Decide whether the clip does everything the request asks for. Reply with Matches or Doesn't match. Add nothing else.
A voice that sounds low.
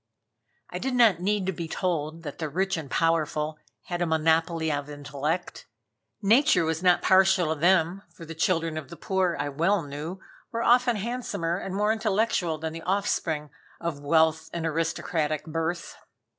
Doesn't match